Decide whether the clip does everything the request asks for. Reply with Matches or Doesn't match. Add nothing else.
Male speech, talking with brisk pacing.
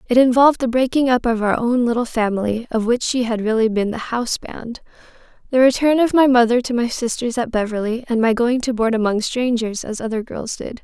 Doesn't match